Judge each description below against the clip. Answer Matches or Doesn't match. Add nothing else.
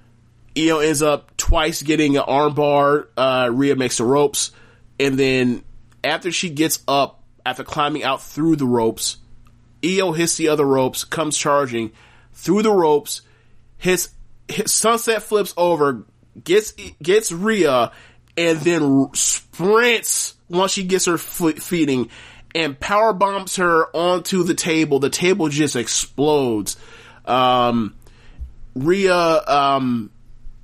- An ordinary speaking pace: Doesn't match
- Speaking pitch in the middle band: Matches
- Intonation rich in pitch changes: Matches